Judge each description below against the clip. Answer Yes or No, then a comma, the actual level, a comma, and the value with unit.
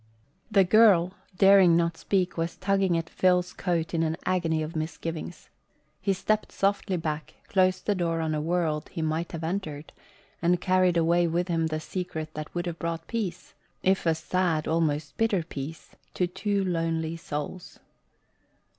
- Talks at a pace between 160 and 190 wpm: Yes, average, 165 wpm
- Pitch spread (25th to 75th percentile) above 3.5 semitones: No, narrow, 2.4 semitones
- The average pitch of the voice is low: No, medium, 170 Hz